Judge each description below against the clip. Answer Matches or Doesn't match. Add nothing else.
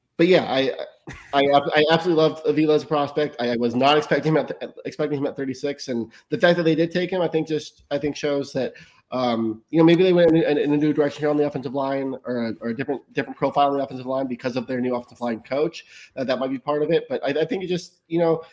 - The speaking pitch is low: Doesn't match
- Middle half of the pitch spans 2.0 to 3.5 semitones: Matches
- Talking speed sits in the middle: Doesn't match